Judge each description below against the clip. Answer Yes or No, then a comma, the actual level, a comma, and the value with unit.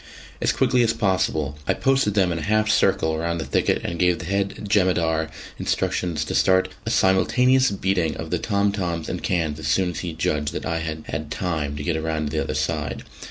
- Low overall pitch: Yes, very low, 85 Hz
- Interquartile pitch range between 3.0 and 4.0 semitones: Yes, average, 3.7 semitones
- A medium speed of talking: No, fast, 215 wpm